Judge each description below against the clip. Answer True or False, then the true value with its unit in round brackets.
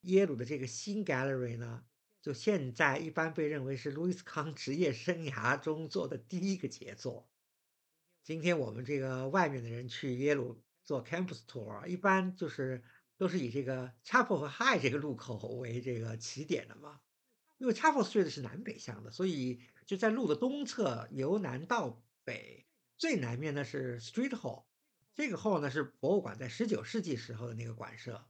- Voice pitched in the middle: True (145 Hz)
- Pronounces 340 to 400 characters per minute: True (345 characters per minute)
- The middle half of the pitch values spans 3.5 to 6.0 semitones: False (6.9 semitones)